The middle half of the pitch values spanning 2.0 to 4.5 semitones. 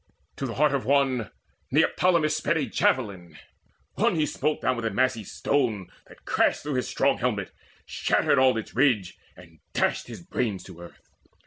No: average, 5.3 semitones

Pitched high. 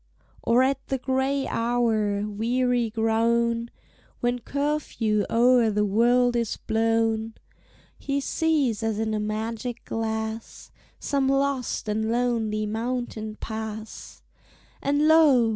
Yes: high, 230 Hz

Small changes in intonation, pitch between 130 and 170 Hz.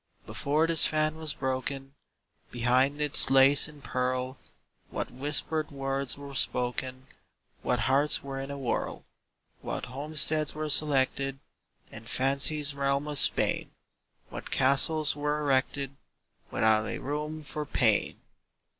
Yes: narrow, 2.2 semitones; medium, 140 Hz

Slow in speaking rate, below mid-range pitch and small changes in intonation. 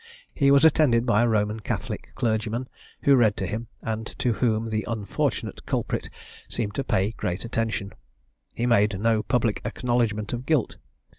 No: average, 160 wpm; low, 115 Hz; narrow, 2.3 semitones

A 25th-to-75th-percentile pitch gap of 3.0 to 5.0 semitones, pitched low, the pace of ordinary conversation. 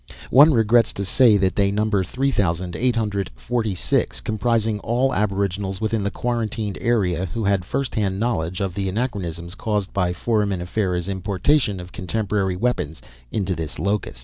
Yes: average, 3.4 semitones; low, 100 Hz; average, 160 wpm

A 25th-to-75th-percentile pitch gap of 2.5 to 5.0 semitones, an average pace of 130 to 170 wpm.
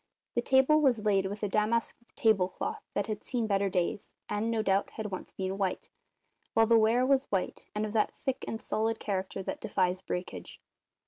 No: average, 2.9 semitones; average, 195 wpm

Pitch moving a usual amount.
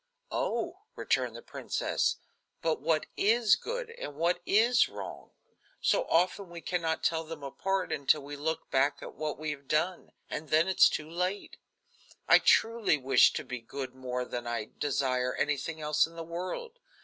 Yes: average, 4.8 semitones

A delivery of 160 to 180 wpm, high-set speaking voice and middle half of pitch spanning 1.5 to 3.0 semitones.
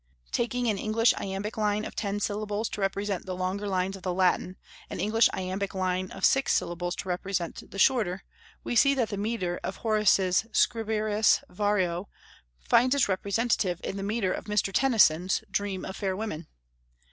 Yes: average, 170 wpm; high, 200 Hz; narrow, 2.6 semitones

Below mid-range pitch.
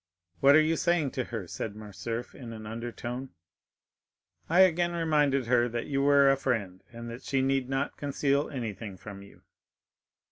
Yes: low, 130 Hz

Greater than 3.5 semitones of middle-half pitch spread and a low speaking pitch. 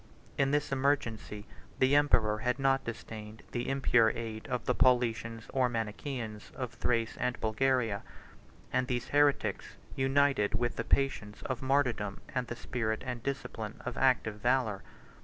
No: average, 3.2 semitones; low, 125 Hz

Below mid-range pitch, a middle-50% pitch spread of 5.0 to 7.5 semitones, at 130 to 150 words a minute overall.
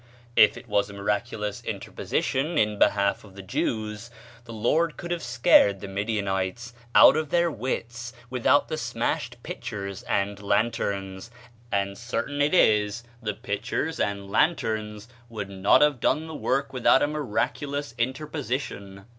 Yes: low, 110 Hz; wide, 5.4 semitones; average, 145 wpm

